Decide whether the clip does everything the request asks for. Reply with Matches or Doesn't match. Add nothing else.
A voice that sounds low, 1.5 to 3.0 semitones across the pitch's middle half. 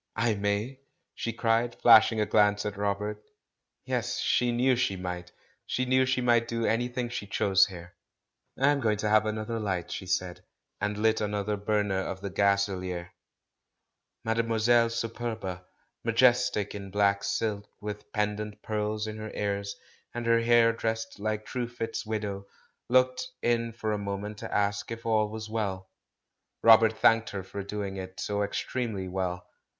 Matches